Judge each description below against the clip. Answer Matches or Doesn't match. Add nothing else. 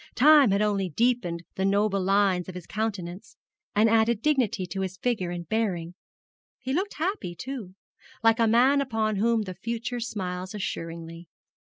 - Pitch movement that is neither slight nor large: Matches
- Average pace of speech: Matches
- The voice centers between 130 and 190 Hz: Doesn't match